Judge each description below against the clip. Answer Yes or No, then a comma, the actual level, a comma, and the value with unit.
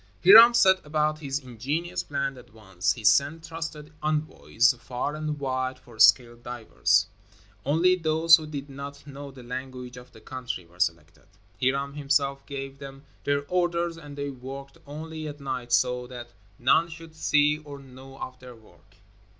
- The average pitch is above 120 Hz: Yes, medium, 140 Hz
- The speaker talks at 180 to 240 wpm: No, average, 165 wpm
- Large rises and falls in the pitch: No, average, 3.3 semitones